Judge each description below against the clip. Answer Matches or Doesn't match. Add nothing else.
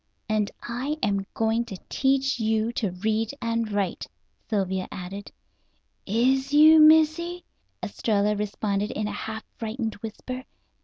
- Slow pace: Matches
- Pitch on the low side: Doesn't match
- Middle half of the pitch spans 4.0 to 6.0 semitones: Matches